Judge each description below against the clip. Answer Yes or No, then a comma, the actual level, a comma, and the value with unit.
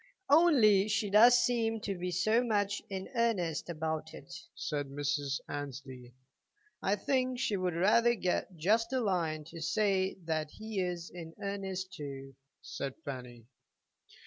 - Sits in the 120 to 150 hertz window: No, medium, 185 Hz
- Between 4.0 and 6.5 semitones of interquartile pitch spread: Yes, wide, 5.6 semitones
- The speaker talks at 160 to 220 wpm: No, average, 145 wpm